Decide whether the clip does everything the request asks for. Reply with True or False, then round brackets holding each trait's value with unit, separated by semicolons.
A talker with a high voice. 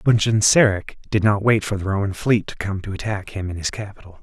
False (100 Hz)